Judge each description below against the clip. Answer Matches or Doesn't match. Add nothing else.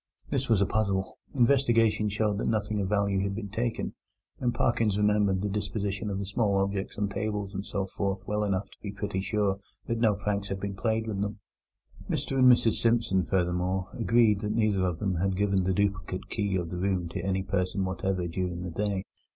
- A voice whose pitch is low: Matches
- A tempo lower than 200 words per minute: Doesn't match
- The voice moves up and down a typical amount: Doesn't match